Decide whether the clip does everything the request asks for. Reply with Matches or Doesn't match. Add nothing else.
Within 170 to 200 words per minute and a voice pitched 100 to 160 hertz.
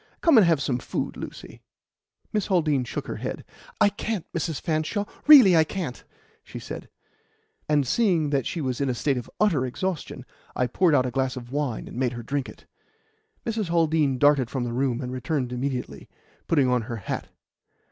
Matches